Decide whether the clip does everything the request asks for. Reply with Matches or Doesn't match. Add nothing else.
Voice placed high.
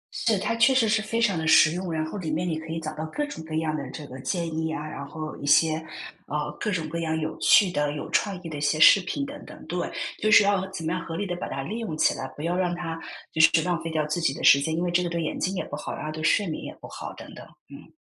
Doesn't match